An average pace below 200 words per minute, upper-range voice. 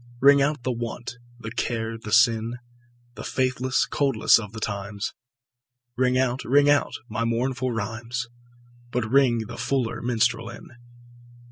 No: average, 140 wpm; low, 120 Hz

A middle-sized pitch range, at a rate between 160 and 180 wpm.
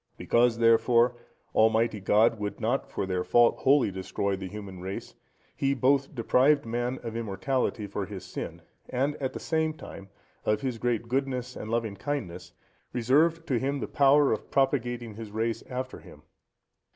Yes: average, 4.0 semitones; average, 165 wpm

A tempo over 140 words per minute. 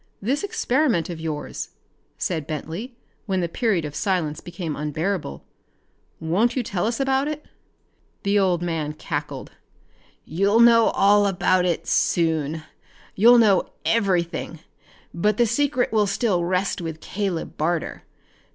No: slow, 135 wpm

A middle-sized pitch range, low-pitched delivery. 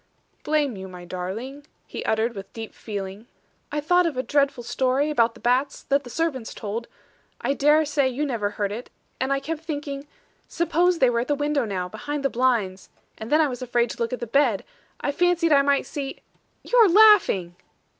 No: average, 4.5 semitones; very high, 265 Hz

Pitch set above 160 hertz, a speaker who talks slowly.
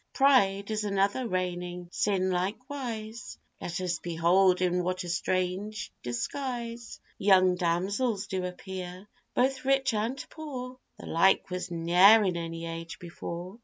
Yes: high, 190 Hz; slow, 130 wpm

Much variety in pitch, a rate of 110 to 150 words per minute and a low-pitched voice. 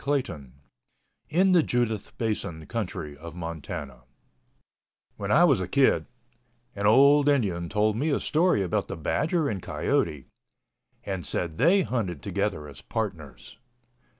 Yes: wide, 8.3 semitones; average, 140 wpm; low, 100 Hz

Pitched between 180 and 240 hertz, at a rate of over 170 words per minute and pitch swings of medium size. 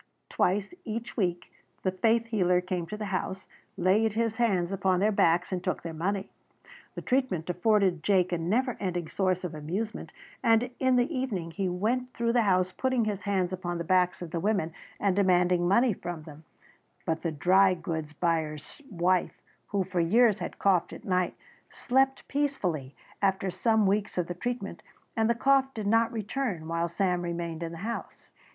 Yes: high, 190 Hz; average, 180 wpm; average, 4.1 semitones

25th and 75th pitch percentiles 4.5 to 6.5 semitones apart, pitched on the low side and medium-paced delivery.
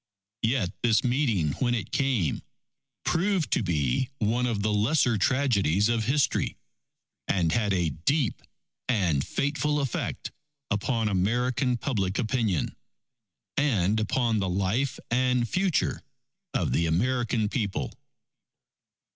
No: average, 4.8 semitones; low, 115 Hz; slow, 115 wpm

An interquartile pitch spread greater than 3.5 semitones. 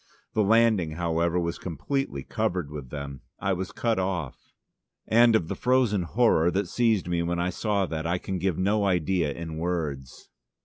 Yes: average, 3.9 semitones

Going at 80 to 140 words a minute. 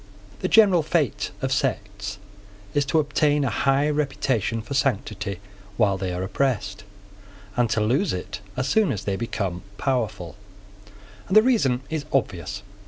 No: average, 150 wpm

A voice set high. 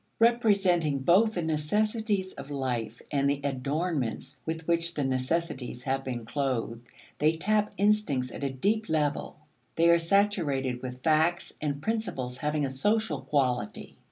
No: medium, 150 Hz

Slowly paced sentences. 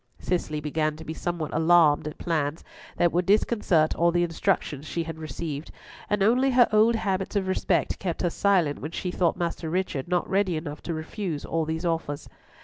No: average, 190 wpm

